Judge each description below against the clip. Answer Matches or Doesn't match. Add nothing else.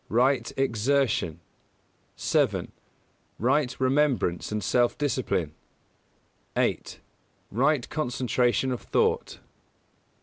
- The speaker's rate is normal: Doesn't match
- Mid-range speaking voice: Doesn't match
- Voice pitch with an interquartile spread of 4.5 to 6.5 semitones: Doesn't match